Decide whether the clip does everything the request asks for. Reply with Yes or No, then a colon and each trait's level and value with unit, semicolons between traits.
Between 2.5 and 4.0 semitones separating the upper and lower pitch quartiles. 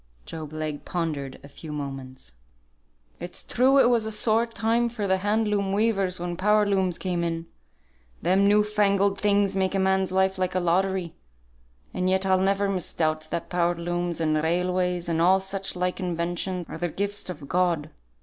Yes: average, 2.8 semitones